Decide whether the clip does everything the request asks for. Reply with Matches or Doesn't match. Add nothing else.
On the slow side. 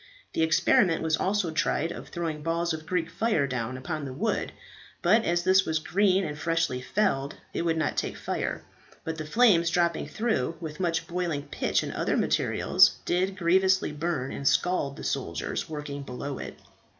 Doesn't match